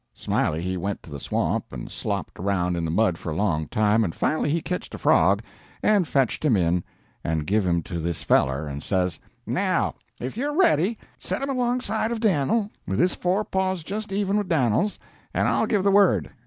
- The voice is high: No, low, 125 Hz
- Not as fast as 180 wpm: No, fast, 205 wpm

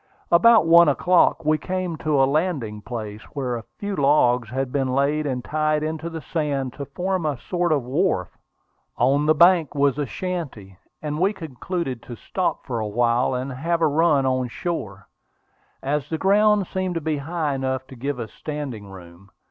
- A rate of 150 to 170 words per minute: No, average, 185 wpm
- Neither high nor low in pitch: Yes, medium, 145 Hz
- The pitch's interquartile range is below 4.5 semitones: No, average, 4.9 semitones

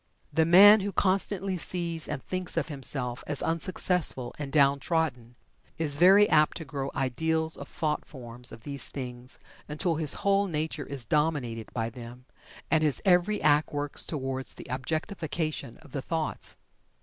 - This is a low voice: No, medium, 150 Hz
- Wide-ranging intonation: No, average, 4.0 semitones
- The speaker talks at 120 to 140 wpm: No, average, 160 wpm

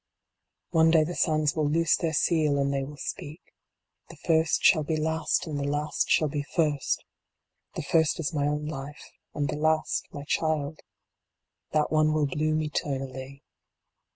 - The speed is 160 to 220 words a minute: Yes, average, 165 wpm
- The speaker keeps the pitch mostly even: Yes, narrow, 1.7 semitones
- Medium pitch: Yes, medium, 150 Hz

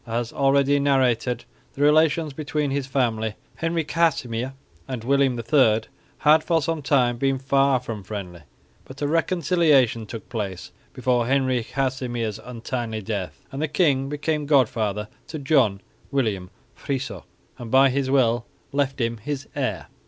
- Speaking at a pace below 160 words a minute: Yes, average, 145 wpm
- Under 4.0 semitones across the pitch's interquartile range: Yes, average, 3.6 semitones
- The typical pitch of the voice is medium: No, low, 130 Hz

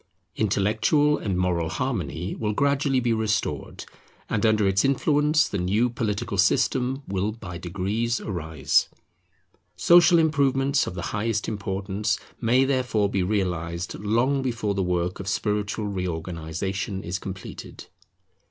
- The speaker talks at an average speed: No, slow, 125 wpm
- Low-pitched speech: Yes, low, 105 Hz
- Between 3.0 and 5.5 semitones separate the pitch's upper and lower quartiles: Yes, average, 4.8 semitones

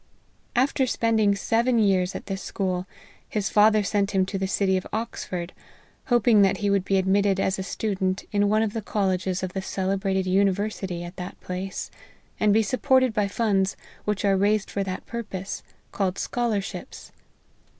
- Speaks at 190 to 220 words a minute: No, average, 170 wpm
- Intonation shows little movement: Yes, narrow, 2.1 semitones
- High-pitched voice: Yes, high, 200 Hz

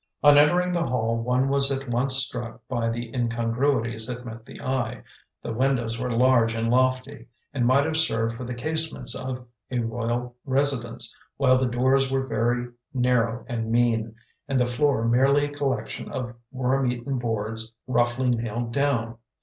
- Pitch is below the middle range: Yes, low, 125 Hz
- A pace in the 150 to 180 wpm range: Yes, average, 165 wpm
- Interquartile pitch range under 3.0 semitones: Yes, narrow, 2.5 semitones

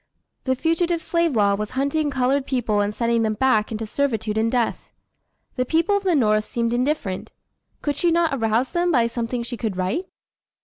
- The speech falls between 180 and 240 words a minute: Yes, average, 185 wpm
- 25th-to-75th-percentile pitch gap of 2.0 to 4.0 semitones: No, average, 5.2 semitones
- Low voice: No, very high, 250 Hz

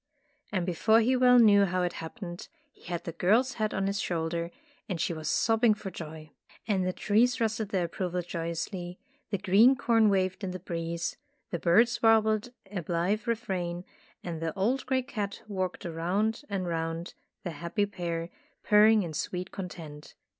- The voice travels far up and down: No, average, 4.1 semitones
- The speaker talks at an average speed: Yes, average, 175 wpm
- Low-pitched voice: No, medium, 185 Hz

